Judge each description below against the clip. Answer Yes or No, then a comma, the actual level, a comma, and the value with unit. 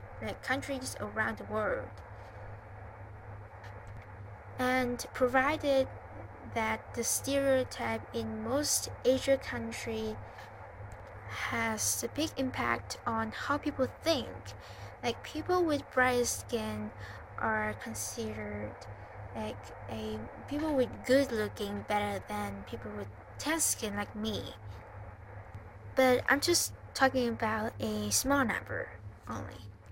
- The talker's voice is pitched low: Yes, low, 110 Hz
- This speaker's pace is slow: Yes, slow, 105 wpm